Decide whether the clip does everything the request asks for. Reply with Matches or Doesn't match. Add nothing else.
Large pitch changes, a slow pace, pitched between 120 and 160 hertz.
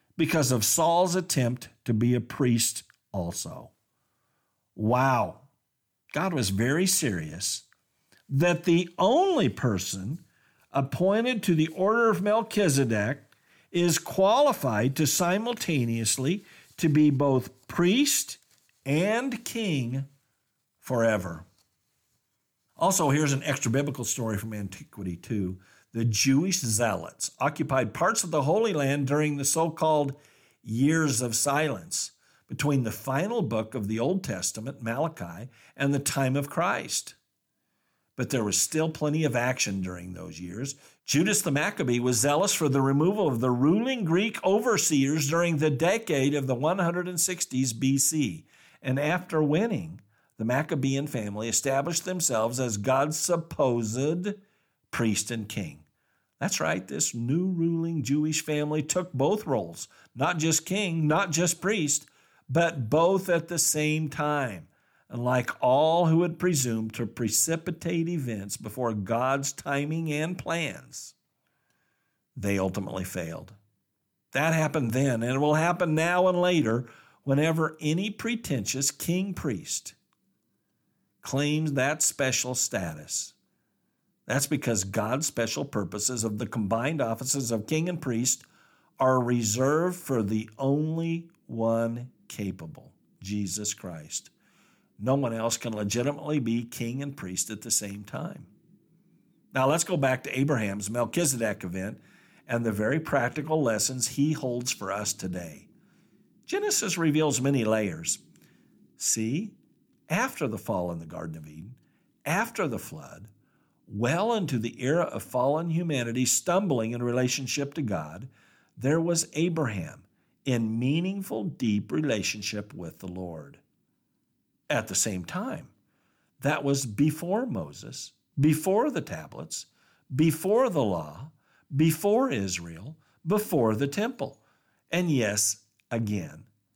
Matches